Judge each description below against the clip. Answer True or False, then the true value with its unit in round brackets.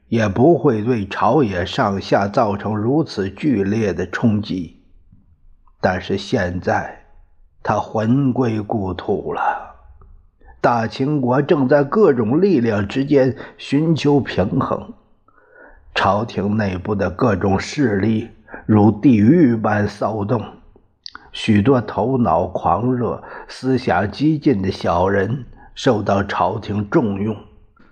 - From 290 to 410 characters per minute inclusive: False (165 characters per minute)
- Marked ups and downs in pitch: False (4.8 semitones)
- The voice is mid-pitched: False (110 Hz)